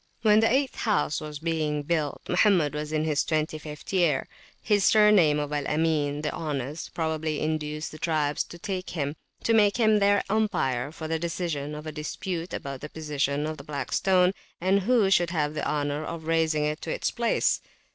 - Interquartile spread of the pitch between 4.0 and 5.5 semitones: No, average, 3.5 semitones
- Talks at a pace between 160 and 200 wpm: Yes, average, 185 wpm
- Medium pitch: Yes, medium, 155 Hz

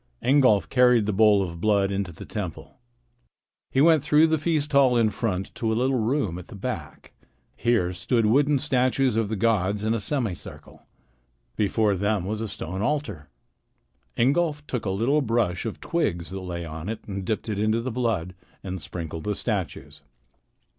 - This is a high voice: No, low, 110 Hz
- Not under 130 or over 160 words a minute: No, average, 175 wpm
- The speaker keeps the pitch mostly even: No, average, 5.0 semitones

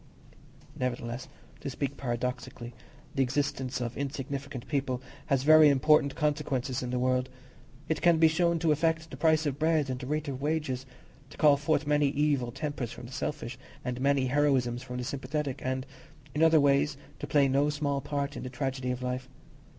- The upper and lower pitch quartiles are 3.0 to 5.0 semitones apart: No, narrow, 2.6 semitones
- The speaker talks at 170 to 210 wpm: Yes, average, 180 wpm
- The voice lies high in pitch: No, medium, 140 Hz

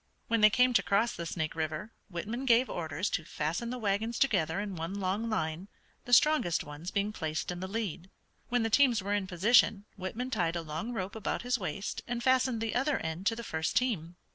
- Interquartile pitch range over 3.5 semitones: Yes, wide, 5.6 semitones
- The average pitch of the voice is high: Yes, high, 200 Hz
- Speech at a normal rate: No, fast, 215 wpm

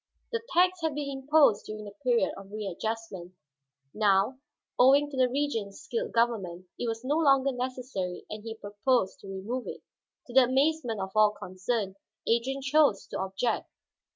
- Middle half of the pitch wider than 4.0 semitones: Yes, average, 4.9 semitones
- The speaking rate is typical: Yes, average, 160 wpm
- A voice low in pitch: No, high, 235 Hz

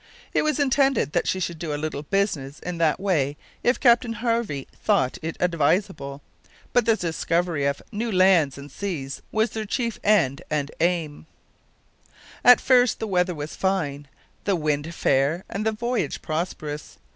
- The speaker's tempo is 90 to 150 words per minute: No, average, 160 wpm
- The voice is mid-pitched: Yes, medium, 175 Hz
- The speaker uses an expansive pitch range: Yes, wide, 6.5 semitones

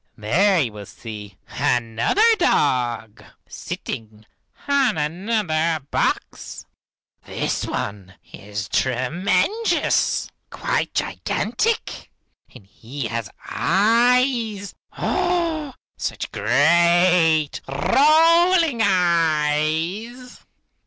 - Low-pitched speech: No, medium, 170 Hz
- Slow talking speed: Yes, slow, 70 wpm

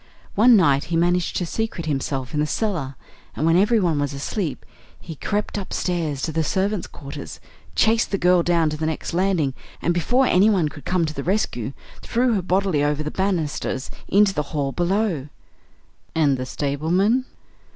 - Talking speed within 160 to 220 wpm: Yes, average, 170 wpm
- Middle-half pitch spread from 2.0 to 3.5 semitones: No, average, 4.9 semitones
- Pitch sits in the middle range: Yes, medium, 170 Hz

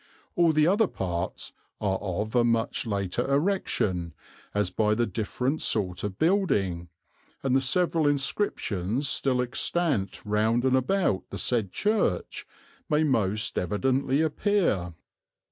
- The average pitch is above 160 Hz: No, low, 120 Hz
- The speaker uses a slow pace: Yes, slow, 130 wpm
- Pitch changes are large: Yes, wide, 7.3 semitones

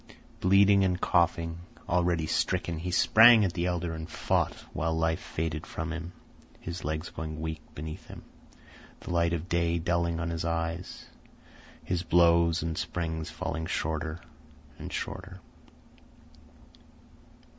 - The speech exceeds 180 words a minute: No, slow, 135 wpm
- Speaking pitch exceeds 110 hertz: No, very low, 85 Hz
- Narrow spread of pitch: Yes, narrow, 1.4 semitones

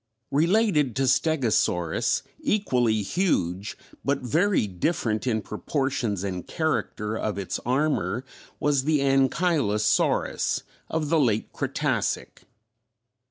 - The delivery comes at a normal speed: No, slow, 100 wpm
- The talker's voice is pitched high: No, low, 130 Hz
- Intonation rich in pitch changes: Yes, wide, 6.6 semitones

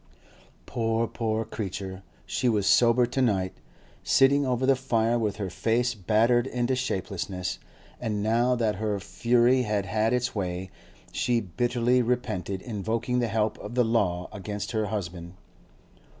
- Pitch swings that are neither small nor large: Yes, average, 3.2 semitones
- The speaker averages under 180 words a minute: Yes, average, 145 wpm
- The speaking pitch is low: Yes, low, 115 Hz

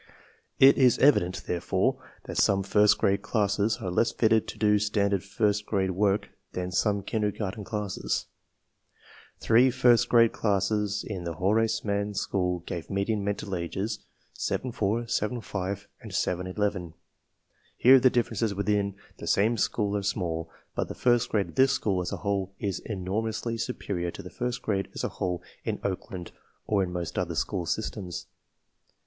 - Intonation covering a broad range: No, average, 2.9 semitones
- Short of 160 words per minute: No, average, 165 wpm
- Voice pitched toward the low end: Yes, low, 100 Hz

